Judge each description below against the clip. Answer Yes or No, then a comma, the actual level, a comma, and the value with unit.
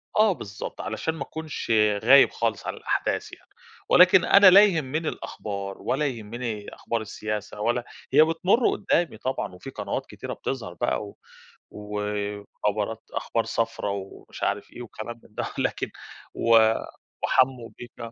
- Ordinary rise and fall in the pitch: No, wide, 5.8 semitones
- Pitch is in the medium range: No, low, 115 Hz